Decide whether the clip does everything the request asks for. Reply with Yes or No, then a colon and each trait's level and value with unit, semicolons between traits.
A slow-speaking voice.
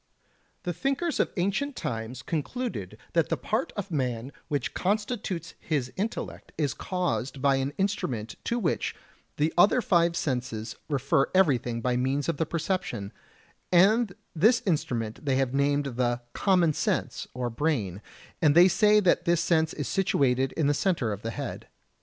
No: average, 160 wpm